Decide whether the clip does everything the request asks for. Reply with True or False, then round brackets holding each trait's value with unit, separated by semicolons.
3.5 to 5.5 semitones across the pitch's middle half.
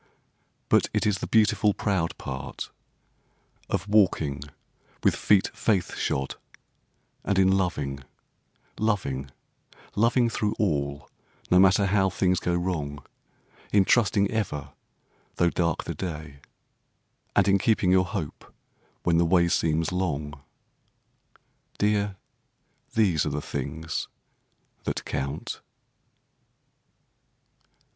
True (5.2 semitones)